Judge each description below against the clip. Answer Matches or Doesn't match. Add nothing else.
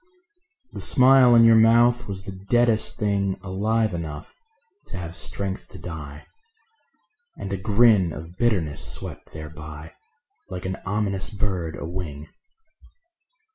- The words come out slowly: Matches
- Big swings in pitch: Doesn't match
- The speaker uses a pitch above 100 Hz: Doesn't match